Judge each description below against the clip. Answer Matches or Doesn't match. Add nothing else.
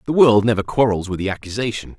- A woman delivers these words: Doesn't match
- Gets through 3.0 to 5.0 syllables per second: Doesn't match